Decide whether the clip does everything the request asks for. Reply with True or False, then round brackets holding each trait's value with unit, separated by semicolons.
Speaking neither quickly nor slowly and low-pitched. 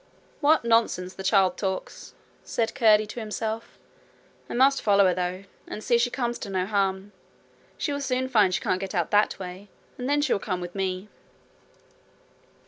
False (185 wpm; 205 Hz)